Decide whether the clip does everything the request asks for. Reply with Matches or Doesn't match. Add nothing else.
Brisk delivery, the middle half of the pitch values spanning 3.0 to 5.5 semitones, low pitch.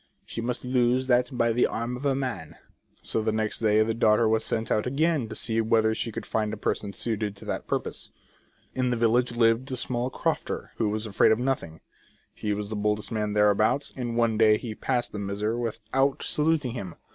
Doesn't match